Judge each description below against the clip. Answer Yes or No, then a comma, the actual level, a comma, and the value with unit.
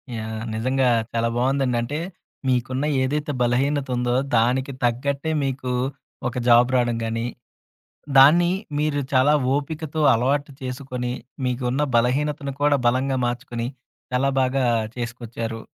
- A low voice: Yes, low, 130 Hz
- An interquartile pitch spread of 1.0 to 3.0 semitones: Yes, narrow, 2.5 semitones